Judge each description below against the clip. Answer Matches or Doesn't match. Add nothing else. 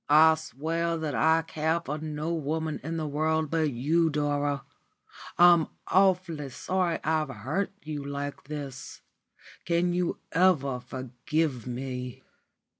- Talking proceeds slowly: Matches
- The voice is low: Doesn't match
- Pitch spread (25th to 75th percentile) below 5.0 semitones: Matches